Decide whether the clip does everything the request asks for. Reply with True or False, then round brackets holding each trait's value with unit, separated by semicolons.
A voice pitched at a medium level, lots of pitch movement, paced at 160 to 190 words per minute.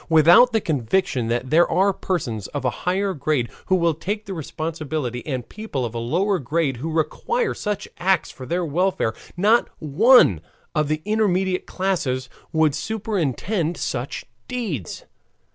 False (165 Hz; 5.7 semitones; 150 wpm)